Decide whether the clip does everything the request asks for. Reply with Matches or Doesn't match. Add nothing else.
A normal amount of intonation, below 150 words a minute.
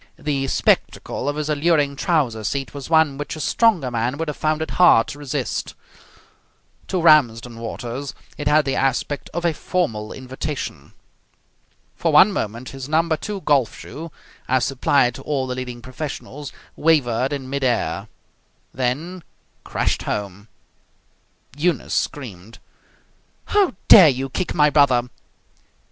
Matches